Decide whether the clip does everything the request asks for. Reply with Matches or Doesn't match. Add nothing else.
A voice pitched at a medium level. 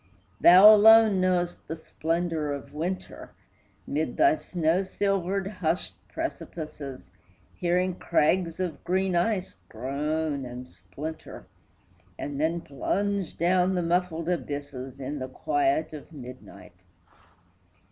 Matches